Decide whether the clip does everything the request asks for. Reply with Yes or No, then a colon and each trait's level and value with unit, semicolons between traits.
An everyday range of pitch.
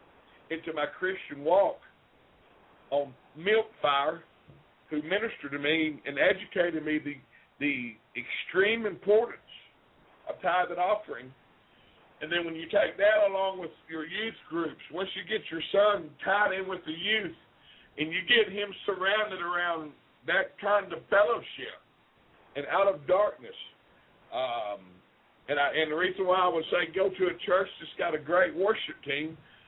Yes: average, 4.4 semitones